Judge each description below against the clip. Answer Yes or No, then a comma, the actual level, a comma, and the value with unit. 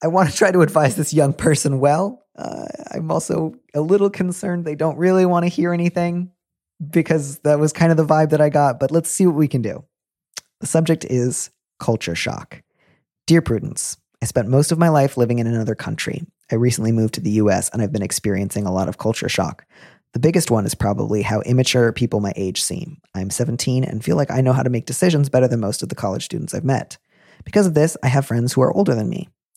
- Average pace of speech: No, fast, 230 wpm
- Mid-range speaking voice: Yes, medium, 145 Hz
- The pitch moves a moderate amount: No, wide, 6.0 semitones